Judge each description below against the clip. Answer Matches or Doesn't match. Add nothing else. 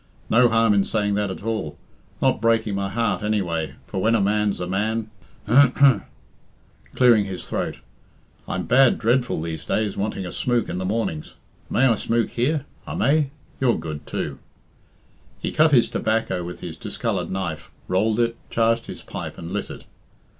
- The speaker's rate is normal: Matches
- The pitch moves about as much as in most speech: Matches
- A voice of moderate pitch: Doesn't match